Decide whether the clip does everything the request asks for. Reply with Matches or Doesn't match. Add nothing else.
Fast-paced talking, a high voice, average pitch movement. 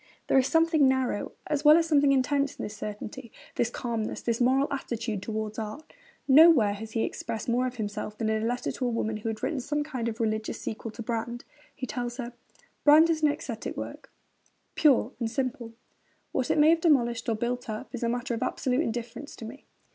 Matches